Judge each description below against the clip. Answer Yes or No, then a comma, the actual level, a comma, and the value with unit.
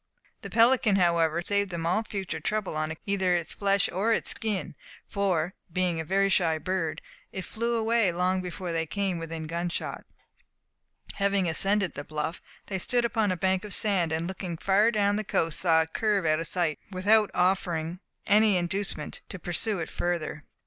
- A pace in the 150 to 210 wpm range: Yes, average, 185 wpm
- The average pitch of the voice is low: No, medium, 185 Hz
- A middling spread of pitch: Yes, average, 3.2 semitones